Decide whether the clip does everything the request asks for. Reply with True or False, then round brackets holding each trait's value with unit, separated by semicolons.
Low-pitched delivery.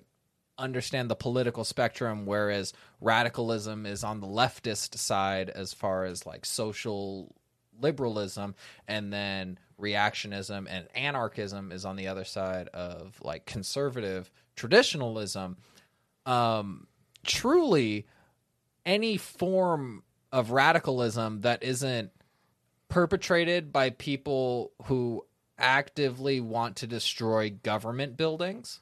True (115 Hz)